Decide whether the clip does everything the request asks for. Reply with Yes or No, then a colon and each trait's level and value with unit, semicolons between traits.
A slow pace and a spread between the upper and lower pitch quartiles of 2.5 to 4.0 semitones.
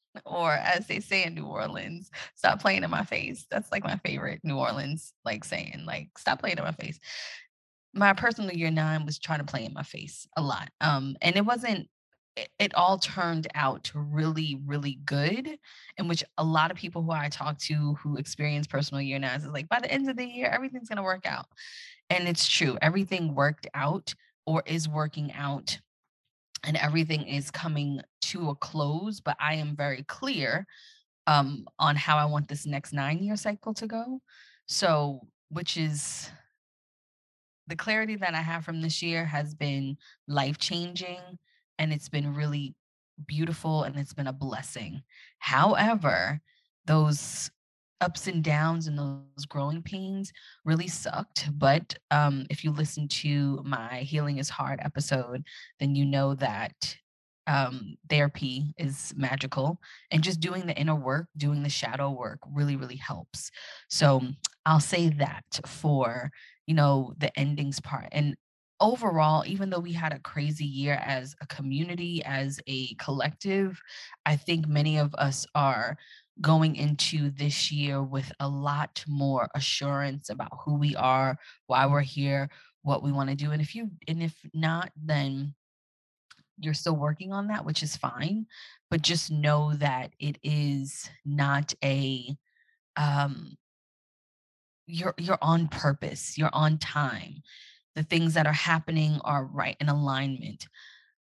No: average, 160 wpm; average, 2.8 semitones